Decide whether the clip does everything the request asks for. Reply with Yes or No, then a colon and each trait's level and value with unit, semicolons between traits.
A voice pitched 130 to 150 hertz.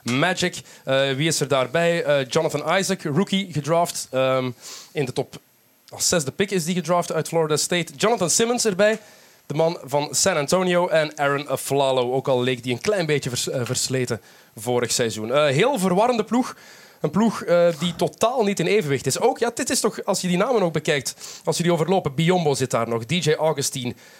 No: medium, 160 Hz